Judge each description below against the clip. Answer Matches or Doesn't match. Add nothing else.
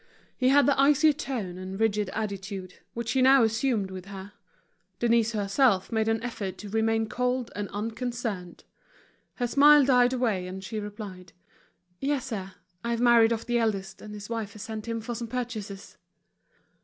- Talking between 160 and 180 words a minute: Matches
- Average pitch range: Matches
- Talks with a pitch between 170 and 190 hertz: Doesn't match